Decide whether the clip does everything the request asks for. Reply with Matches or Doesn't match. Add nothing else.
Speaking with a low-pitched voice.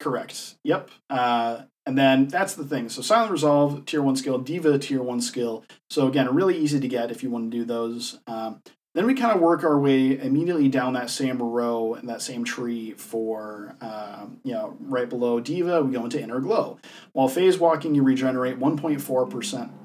Matches